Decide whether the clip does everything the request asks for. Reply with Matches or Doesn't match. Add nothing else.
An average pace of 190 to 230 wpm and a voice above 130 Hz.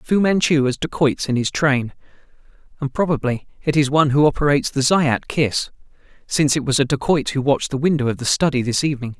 Matches